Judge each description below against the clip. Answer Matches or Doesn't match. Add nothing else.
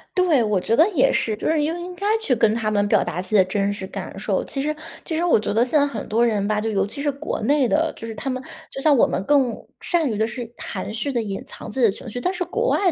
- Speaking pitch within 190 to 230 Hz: Doesn't match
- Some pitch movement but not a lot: Doesn't match